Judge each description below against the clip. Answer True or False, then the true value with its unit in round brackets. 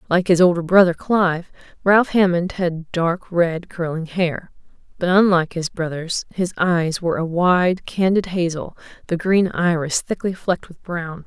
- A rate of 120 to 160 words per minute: True (155 wpm)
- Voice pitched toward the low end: False (175 Hz)